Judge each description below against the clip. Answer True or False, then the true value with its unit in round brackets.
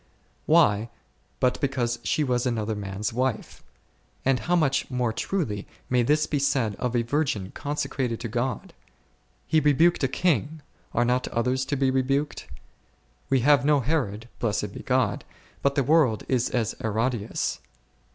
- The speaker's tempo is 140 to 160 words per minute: True (155 wpm)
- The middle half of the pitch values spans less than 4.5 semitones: True (3.8 semitones)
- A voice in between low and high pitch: False (130 Hz)